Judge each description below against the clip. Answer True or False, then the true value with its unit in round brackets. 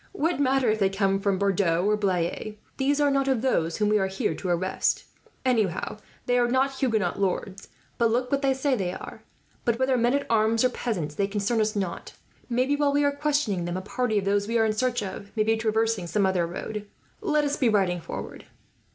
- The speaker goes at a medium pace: False (220 wpm)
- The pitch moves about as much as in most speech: True (4.9 semitones)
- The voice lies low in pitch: False (220 Hz)